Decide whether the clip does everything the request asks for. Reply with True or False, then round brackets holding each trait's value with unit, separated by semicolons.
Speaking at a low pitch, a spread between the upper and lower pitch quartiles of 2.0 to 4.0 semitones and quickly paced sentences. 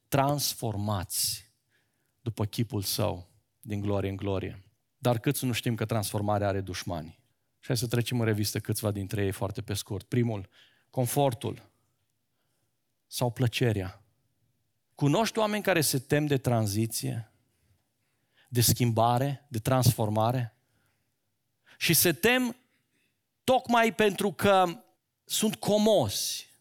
False (120 Hz; 3.7 semitones; 115 wpm)